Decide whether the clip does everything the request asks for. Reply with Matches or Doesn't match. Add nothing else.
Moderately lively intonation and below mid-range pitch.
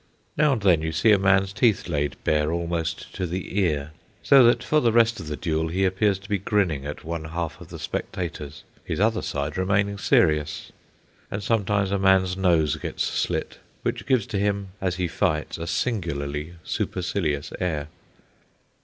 Matches